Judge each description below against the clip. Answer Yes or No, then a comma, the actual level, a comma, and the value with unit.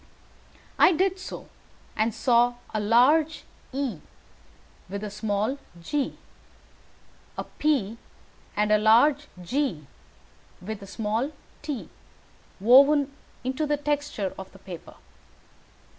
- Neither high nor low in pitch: No, high, 240 Hz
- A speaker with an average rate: No, slow, 110 wpm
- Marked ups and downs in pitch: Yes, wide, 5.7 semitones